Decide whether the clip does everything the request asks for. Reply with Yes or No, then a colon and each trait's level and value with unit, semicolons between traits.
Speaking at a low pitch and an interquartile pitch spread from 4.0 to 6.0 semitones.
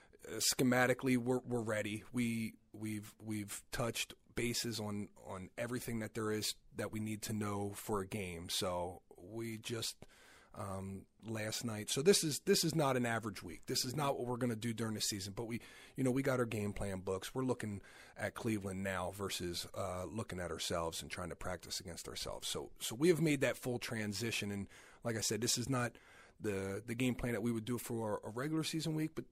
No: low, 110 Hz; average, 3.4 semitones